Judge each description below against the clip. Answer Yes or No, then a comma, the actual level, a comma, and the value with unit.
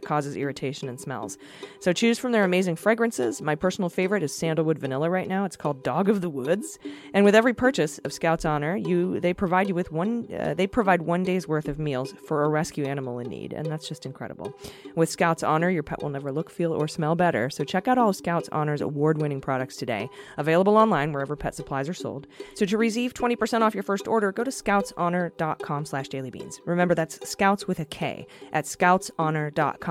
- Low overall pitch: No, medium, 165 Hz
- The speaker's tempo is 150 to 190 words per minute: No, fast, 205 wpm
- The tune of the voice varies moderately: Yes, average, 4.8 semitones